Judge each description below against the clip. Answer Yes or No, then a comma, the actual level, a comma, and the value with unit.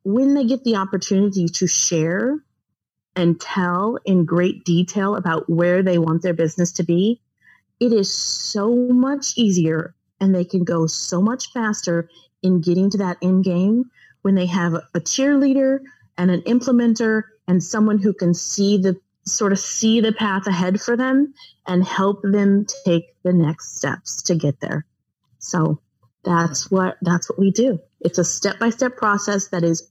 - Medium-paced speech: Yes, average, 170 wpm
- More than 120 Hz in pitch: Yes, high, 190 Hz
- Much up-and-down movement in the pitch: No, average, 4.0 semitones